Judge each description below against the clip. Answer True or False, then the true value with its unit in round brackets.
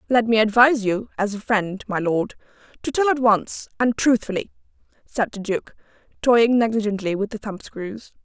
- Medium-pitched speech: False (220 Hz)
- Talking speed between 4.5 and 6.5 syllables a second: True (5.0 syllables/s)